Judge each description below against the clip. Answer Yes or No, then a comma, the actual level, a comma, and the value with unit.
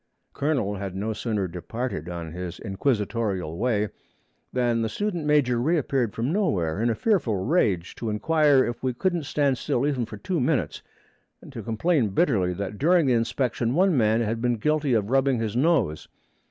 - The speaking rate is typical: Yes, average, 175 wpm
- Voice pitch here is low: Yes, low, 120 Hz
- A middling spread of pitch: No, wide, 5.7 semitones